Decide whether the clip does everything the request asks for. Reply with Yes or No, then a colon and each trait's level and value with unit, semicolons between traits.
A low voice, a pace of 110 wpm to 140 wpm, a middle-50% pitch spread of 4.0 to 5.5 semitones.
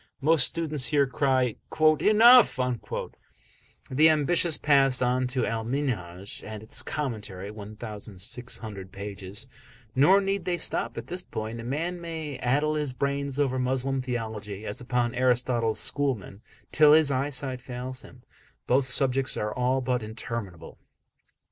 Yes: low, 130 Hz; slow, 135 wpm; average, 4.3 semitones